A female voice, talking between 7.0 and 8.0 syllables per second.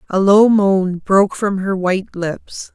No: female; 3.9 syllables/s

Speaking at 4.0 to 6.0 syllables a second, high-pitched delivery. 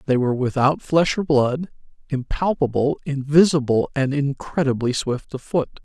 No: 4.8 syllables/s; medium, 140 Hz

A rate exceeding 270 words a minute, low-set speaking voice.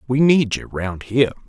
No: fast, 205 wpm; low, 120 Hz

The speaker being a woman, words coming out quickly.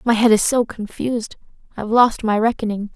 No: female; average, 185 wpm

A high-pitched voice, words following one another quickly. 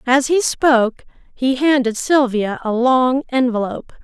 No: very high, 255 Hz; slow, 135 wpm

